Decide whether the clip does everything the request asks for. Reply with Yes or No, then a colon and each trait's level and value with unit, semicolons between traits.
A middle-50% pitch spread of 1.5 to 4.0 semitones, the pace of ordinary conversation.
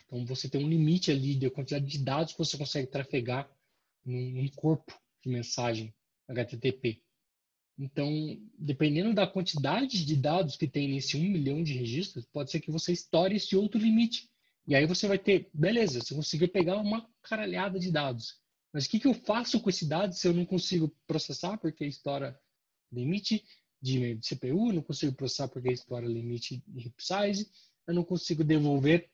No: average, 5.2 semitones; average, 175 wpm